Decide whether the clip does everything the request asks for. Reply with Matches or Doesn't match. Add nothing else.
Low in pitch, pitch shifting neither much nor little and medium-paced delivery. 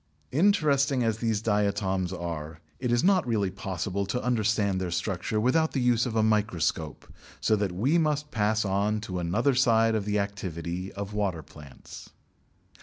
Matches